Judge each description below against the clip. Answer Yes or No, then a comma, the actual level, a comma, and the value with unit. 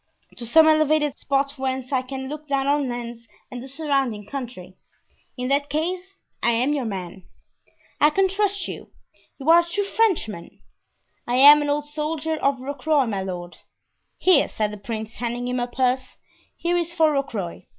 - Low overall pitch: No, very high, 275 Hz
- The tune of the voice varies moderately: Yes, average, 4.2 semitones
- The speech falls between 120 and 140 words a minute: No, average, 170 wpm